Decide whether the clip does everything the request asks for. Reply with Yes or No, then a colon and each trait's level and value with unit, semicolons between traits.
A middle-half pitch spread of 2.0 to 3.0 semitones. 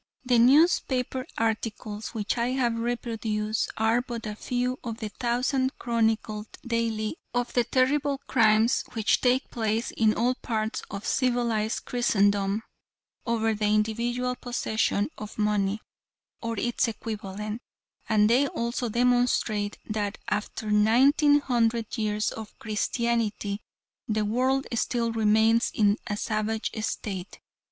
Yes: narrow, 2.4 semitones